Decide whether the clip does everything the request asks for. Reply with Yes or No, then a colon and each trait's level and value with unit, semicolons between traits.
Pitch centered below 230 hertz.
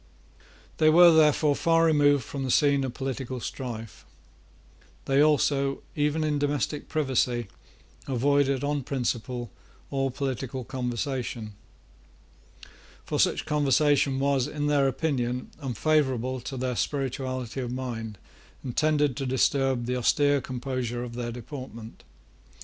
Yes: low, 135 Hz